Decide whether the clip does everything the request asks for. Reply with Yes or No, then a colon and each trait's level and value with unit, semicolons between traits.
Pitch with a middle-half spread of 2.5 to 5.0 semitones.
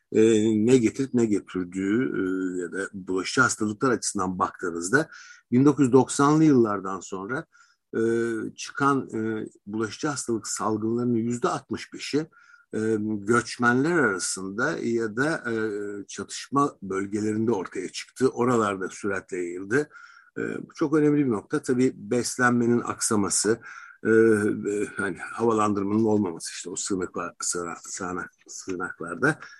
Yes: average, 4.0 semitones